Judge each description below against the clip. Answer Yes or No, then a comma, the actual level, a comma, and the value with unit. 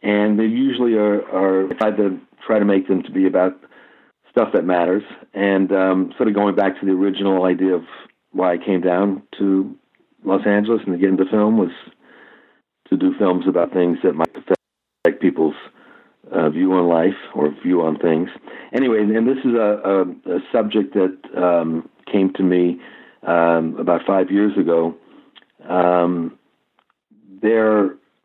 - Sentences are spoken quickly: No, average, 170 wpm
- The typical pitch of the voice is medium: No, very low, 95 Hz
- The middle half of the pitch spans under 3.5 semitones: Yes, narrow, 2.5 semitones